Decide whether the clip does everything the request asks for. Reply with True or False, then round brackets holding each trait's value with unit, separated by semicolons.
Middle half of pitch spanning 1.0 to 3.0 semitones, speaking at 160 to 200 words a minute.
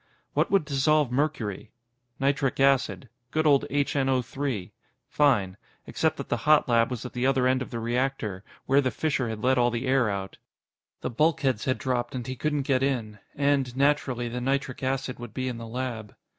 True (2.6 semitones; 185 wpm)